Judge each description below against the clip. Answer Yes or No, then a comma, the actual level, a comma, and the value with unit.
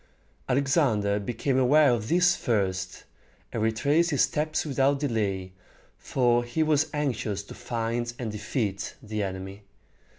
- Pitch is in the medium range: No, low, 120 Hz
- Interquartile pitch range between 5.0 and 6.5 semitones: Yes, average, 5.3 semitones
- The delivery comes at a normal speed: No, slow, 130 wpm